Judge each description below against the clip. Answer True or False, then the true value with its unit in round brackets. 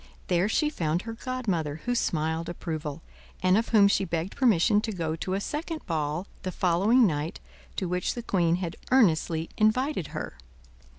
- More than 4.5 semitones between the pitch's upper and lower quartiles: True (5.5 semitones)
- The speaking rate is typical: True (170 wpm)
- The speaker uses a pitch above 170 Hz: True (185 Hz)